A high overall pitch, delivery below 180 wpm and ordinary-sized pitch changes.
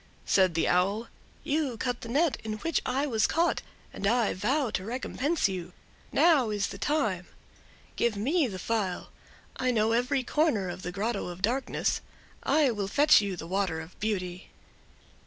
No: high, 220 Hz; average, 165 wpm; wide, 5.9 semitones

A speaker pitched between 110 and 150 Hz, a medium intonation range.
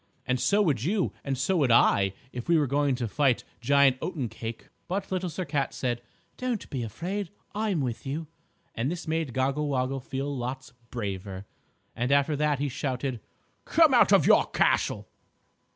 Yes: low, 135 Hz; average, 4.3 semitones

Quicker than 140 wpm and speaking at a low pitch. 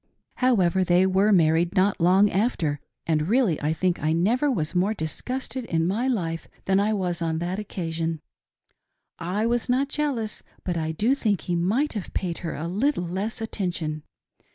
No: average, 175 wpm; medium, 185 Hz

